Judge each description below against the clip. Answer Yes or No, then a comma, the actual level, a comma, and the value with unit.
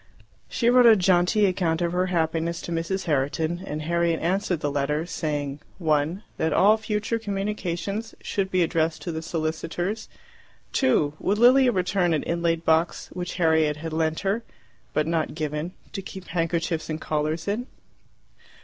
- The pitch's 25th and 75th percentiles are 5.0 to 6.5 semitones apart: No, average, 3.4 semitones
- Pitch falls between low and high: Yes, medium, 170 Hz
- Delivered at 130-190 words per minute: Yes, average, 160 wpm